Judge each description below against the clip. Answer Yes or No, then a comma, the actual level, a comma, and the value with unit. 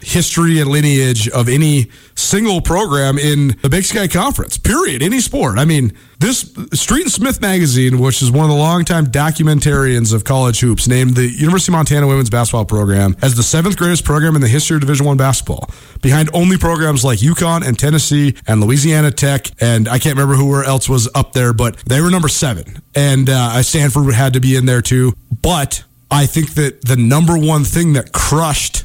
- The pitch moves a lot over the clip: No, average, 3.9 semitones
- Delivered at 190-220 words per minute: Yes, average, 200 wpm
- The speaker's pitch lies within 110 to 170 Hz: Yes, medium, 140 Hz